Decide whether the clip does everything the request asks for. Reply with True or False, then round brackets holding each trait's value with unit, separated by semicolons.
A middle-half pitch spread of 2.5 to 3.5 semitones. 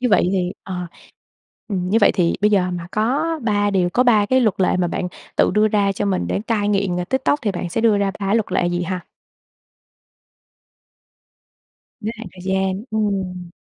True (2.8 semitones)